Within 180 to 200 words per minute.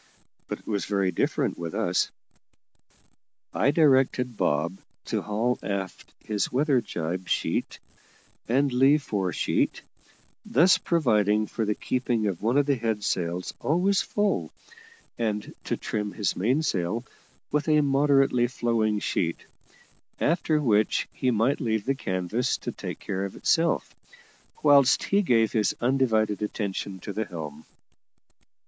No: slow, 135 wpm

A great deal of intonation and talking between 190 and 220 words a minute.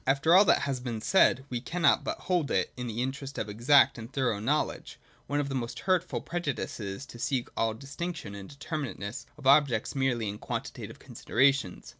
No: average, 3.8 semitones; average, 200 wpm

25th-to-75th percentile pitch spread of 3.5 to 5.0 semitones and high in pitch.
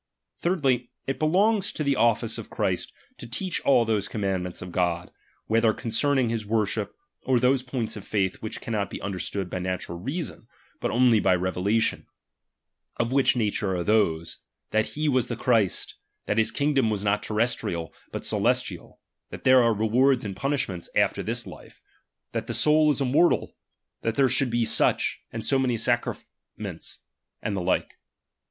No: average, 4.7 semitones; low, 115 Hz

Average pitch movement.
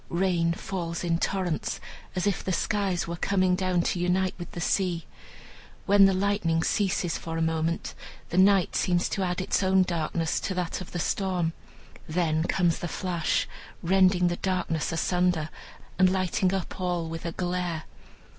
No: narrow, 2.0 semitones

